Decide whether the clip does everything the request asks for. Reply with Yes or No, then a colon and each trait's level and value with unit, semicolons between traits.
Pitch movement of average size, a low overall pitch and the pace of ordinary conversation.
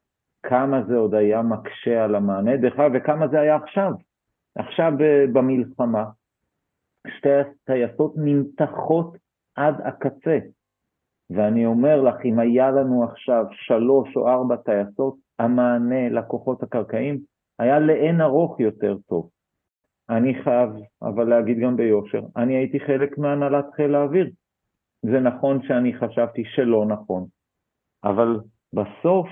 Yes: average, 3.7 semitones; low, 125 Hz; average, 120 wpm